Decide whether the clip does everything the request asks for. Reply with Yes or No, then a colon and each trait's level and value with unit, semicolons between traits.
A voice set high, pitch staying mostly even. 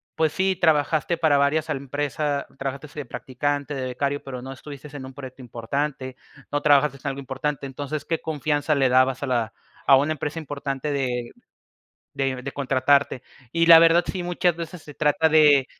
No: medium, 140 Hz; narrow, 2.3 semitones